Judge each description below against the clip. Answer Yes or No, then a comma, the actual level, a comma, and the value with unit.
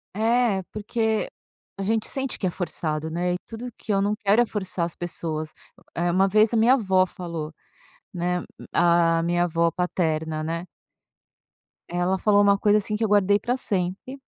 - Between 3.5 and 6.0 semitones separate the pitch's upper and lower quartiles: Yes, average, 3.8 semitones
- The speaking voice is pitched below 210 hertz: Yes, high, 190 Hz